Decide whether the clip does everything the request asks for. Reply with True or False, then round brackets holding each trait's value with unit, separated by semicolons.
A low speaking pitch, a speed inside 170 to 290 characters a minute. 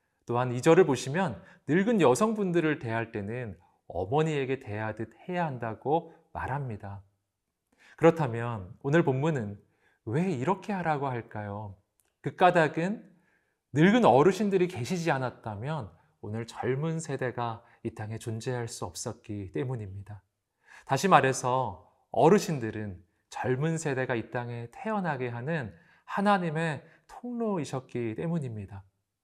True (125 Hz; 270 characters per minute)